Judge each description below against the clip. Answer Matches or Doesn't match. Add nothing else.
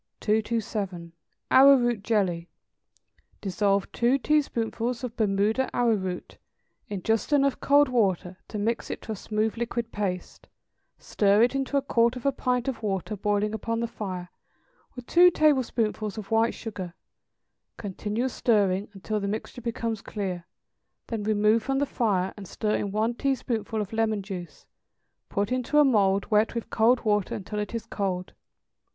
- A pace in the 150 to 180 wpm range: Matches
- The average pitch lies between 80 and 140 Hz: Doesn't match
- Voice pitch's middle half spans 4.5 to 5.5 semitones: Doesn't match